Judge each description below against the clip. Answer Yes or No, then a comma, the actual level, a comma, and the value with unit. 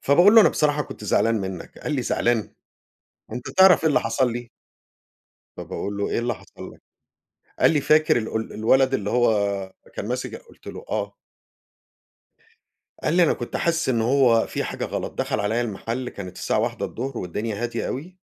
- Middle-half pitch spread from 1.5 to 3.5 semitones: No, average, 4.6 semitones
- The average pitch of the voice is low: Yes, low, 120 Hz